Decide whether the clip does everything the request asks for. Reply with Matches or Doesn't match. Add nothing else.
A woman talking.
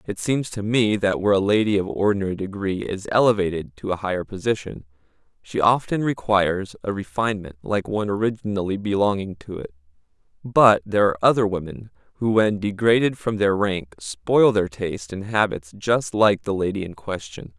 Doesn't match